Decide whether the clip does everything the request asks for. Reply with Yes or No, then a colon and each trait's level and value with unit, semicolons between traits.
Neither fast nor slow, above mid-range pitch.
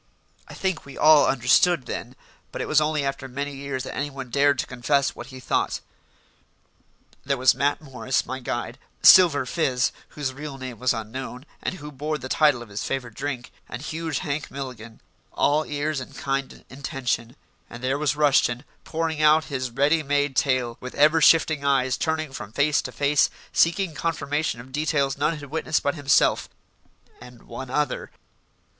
No: average, 175 wpm; medium, 140 Hz